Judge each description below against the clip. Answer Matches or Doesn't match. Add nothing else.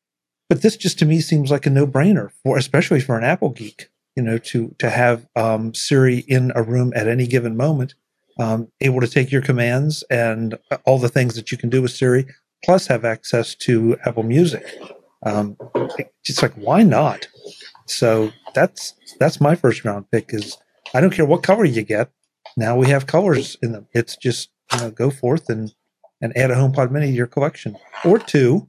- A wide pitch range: Doesn't match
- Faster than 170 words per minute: Matches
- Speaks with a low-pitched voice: Matches